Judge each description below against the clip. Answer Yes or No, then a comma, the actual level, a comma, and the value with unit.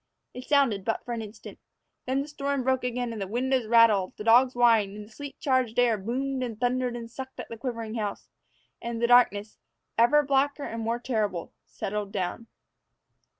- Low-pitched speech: No, high, 235 Hz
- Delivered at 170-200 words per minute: Yes, average, 175 wpm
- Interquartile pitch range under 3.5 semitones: Yes, average, 3.0 semitones